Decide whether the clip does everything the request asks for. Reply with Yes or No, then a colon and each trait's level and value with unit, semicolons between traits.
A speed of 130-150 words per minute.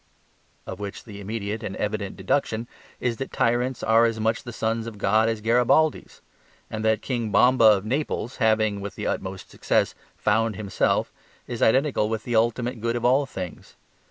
No: average, 175 wpm